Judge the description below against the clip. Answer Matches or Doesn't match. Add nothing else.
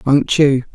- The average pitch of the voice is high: Doesn't match